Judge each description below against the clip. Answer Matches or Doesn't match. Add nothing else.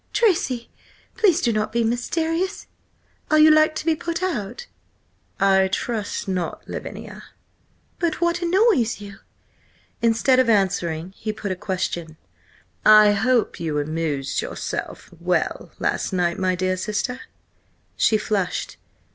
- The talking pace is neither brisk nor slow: Doesn't match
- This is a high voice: Matches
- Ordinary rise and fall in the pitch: Doesn't match